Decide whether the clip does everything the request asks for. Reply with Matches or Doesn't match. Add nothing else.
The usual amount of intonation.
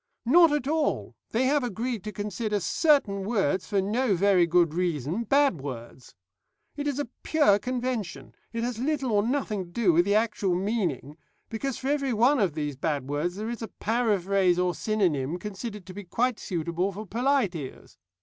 Doesn't match